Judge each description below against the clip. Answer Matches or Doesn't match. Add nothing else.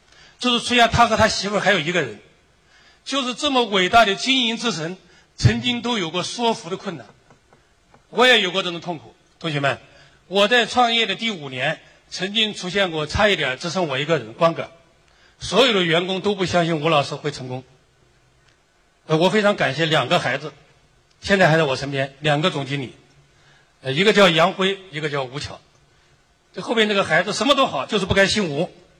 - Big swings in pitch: Matches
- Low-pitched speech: Doesn't match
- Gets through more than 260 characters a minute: Matches